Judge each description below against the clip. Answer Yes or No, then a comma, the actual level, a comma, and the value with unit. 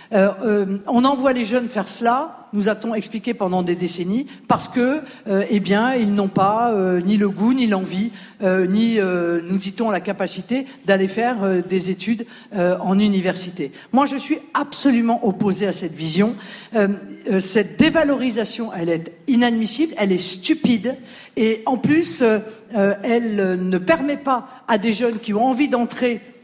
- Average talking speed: Yes, average, 175 wpm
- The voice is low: No, high, 215 Hz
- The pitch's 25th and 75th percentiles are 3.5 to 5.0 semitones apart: Yes, average, 4.1 semitones